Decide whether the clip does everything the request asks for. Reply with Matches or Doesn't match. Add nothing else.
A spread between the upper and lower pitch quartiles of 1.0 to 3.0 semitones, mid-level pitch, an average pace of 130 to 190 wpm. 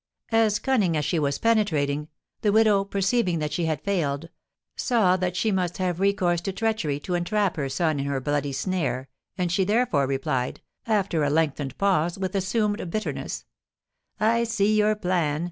Doesn't match